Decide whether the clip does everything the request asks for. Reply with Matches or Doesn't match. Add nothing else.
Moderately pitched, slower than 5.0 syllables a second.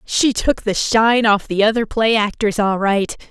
Doesn't match